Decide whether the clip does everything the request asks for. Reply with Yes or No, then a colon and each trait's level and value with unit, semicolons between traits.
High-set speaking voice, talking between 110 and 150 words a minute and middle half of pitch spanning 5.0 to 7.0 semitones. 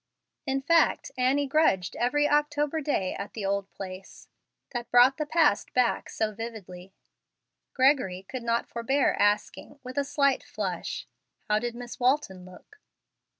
Yes: high, 245 Hz; average, 145 wpm; wide, 5.6 semitones